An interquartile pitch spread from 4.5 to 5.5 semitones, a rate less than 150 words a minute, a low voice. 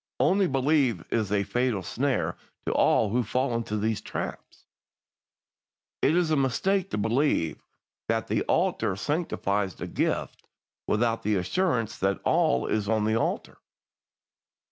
Yes: average, 5.1 semitones; average, 140 wpm; low, 115 Hz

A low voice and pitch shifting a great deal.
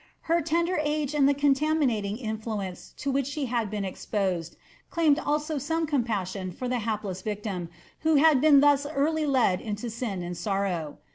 No: very high, 250 Hz; wide, 6.6 semitones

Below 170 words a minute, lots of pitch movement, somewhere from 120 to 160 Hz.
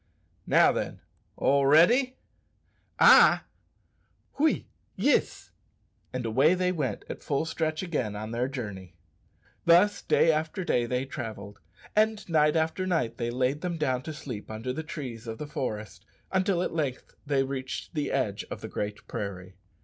Yes: average, 155 wpm; wide, 5.9 semitones; low, 135 Hz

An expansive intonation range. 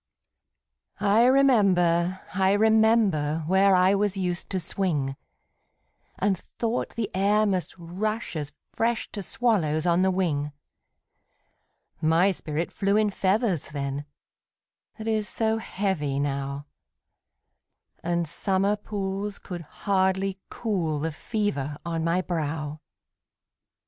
No: average, 4.2 semitones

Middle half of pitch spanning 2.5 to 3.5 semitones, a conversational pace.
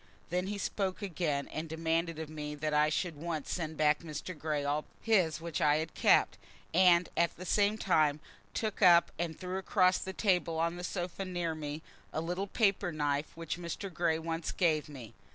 No: average, 2.9 semitones; fast, 210 wpm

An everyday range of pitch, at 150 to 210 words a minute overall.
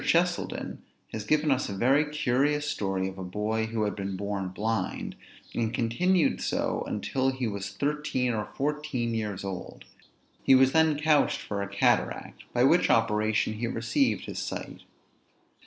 No: wide, 5.9 semitones; average, 155 wpm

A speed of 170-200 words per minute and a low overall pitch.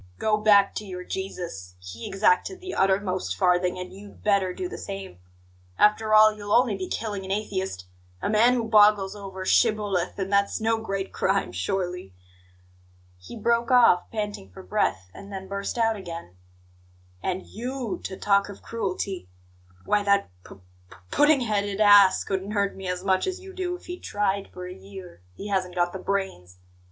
No: average, 175 wpm; high, 200 Hz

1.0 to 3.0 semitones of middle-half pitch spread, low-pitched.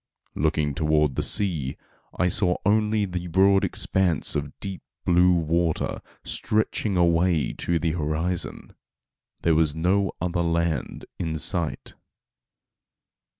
Yes: average, 2.7 semitones; very low, 85 Hz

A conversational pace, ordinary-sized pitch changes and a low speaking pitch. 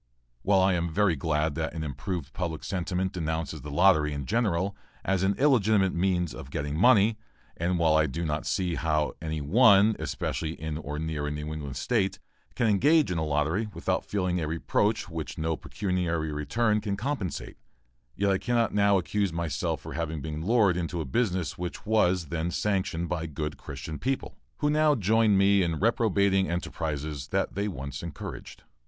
Yes: average, 180 wpm; average, 4.4 semitones; very low, 90 Hz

